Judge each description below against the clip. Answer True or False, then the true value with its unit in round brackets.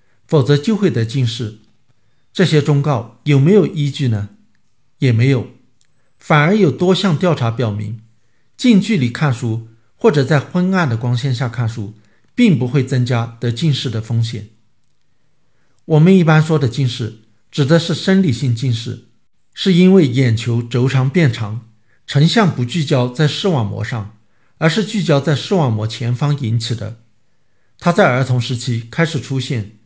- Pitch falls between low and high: False (130 Hz)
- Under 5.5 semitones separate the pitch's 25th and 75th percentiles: True (5.1 semitones)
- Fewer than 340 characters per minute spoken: True (230 characters per minute)